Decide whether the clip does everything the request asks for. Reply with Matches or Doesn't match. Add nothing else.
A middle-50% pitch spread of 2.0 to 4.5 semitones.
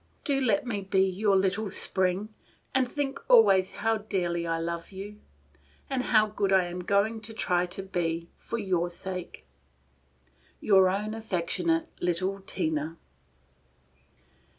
Matches